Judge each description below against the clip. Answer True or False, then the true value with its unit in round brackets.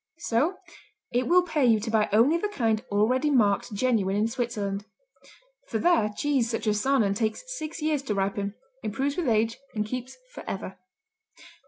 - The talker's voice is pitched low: False (230 Hz)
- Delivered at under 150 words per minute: False (165 wpm)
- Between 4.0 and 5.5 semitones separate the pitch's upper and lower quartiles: True (4.7 semitones)